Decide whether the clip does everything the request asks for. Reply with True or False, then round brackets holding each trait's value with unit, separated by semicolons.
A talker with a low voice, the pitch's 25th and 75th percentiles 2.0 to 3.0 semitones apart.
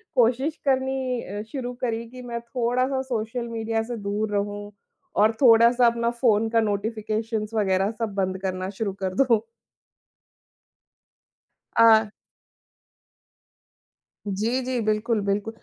False (225 Hz; 2.7 semitones)